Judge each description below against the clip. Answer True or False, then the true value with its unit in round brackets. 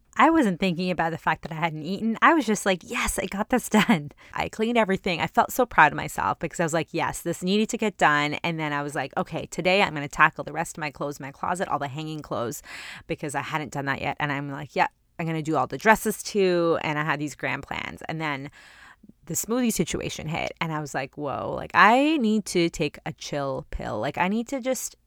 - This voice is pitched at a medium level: True (170 Hz)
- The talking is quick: True (260 wpm)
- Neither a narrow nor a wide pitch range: False (5.7 semitones)